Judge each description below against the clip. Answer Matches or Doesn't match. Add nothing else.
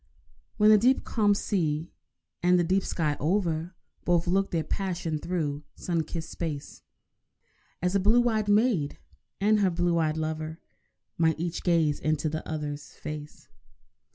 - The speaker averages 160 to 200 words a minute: Doesn't match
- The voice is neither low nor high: Matches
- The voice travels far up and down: Doesn't match